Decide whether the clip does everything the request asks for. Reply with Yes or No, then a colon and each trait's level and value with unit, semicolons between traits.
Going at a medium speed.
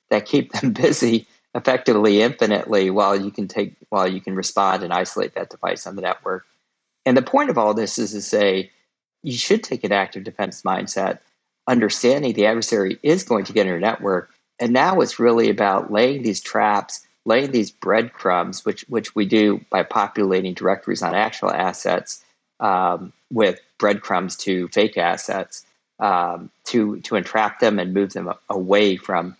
Yes: average, 170 wpm